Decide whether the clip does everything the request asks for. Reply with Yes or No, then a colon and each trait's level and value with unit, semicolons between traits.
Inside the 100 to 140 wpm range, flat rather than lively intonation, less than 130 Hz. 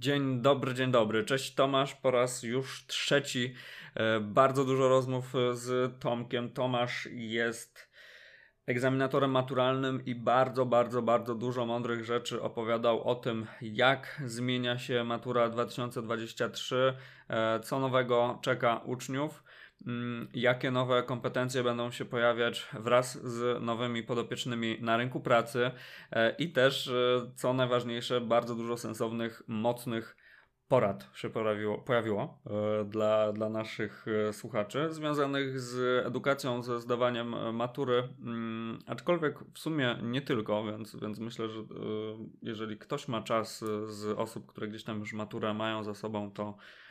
Yes: average, 125 wpm; narrow, 2.1 semitones; low, 120 Hz